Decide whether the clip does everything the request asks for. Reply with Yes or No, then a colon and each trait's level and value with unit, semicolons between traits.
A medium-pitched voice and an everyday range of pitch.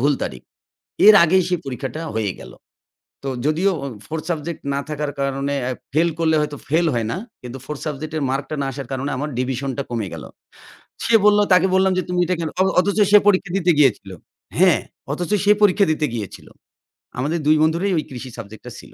Yes: medium, 150 Hz; average, 4.5 semitones